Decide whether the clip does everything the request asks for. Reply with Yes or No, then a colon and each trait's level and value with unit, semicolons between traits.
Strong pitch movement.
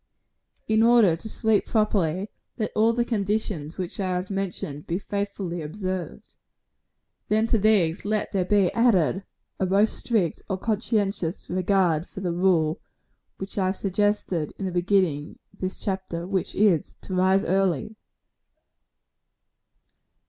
No: average, 2.9 semitones